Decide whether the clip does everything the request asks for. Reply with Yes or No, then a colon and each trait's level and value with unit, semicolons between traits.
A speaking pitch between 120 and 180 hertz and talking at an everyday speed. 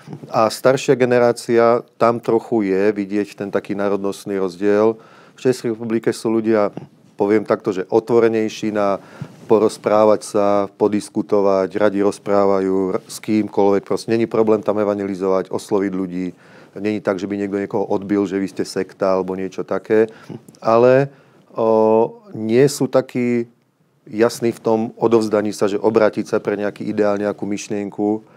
No: low, 105 Hz; average, 140 wpm